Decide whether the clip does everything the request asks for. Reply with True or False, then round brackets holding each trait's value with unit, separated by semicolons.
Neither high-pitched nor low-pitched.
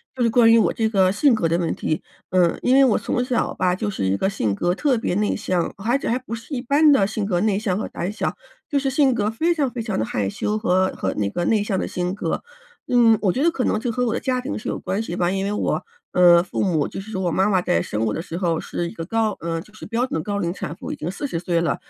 False (205 Hz)